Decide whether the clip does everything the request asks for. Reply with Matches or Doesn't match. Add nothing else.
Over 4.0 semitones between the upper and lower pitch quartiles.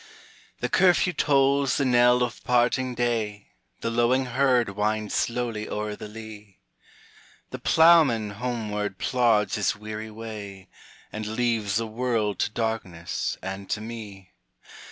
Doesn't match